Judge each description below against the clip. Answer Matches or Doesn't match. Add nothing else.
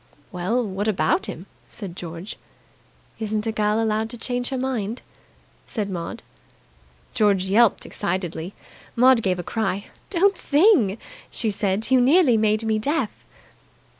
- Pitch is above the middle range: Matches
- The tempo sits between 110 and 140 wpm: Matches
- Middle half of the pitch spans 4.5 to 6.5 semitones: Doesn't match